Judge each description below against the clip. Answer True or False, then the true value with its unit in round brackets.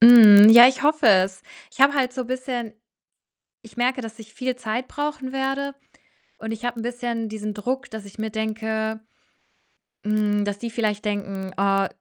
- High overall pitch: True (225 Hz)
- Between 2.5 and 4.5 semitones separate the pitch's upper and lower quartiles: True (3.2 semitones)